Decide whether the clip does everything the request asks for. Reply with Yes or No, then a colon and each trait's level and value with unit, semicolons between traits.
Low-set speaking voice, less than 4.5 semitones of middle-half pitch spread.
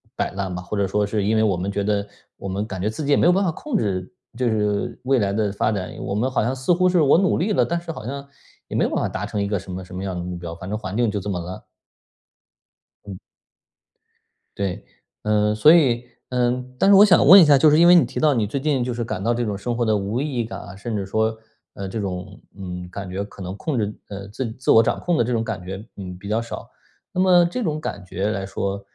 No: low, 110 Hz; average, 5.2 semitones